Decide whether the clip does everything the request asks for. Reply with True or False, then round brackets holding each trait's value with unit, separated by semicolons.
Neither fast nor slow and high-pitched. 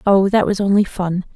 False (220 wpm; 195 Hz)